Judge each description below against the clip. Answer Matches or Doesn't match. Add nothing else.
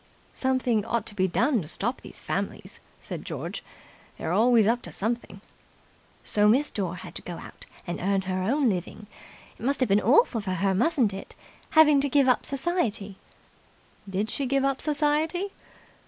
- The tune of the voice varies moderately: Doesn't match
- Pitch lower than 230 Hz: Doesn't match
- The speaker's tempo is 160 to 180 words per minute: Matches